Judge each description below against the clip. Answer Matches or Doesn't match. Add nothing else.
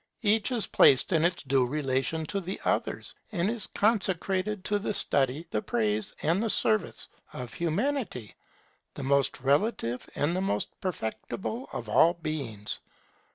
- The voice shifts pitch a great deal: Matches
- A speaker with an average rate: Matches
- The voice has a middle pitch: Matches